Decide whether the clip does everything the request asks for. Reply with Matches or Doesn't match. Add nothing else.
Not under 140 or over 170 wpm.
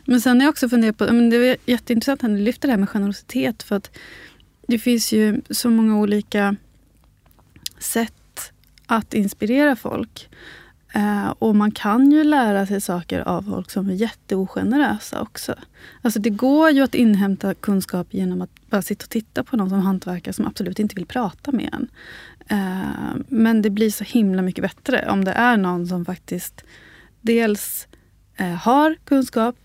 Matches